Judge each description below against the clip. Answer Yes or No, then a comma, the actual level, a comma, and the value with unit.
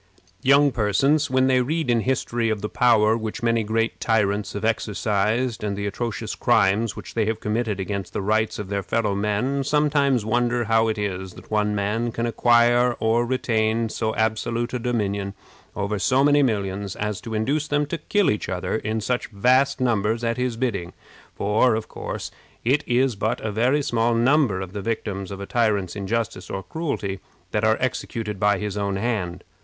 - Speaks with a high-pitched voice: No, low, 110 Hz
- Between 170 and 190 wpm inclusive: Yes, average, 185 wpm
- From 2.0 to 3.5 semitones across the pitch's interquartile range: Yes, average, 3.0 semitones